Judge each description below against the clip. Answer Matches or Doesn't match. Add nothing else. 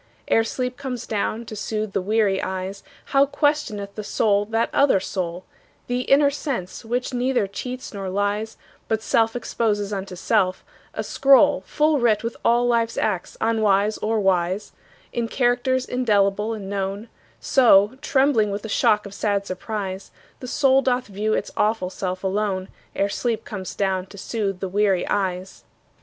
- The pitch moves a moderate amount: Matches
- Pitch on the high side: Matches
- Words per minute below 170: Matches